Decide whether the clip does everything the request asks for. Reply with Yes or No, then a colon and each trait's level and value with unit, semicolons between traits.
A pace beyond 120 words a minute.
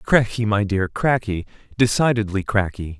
No: slow, 100 wpm